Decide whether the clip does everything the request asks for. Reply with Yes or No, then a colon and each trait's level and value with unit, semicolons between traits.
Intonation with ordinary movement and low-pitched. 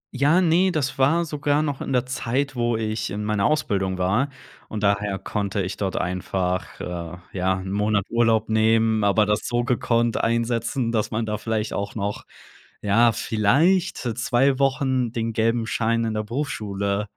Yes: average, 3.7 semitones; low, 115 Hz